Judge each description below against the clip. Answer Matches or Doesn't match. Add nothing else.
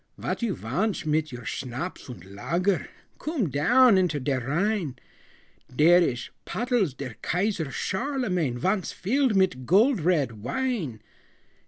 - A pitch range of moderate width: Doesn't match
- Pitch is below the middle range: Doesn't match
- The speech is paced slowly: Matches